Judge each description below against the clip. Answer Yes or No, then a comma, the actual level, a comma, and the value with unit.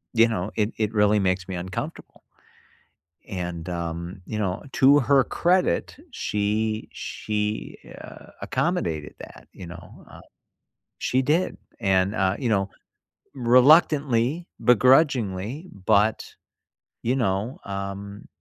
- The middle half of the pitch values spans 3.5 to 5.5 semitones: Yes, average, 5.0 semitones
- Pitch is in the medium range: No, low, 105 Hz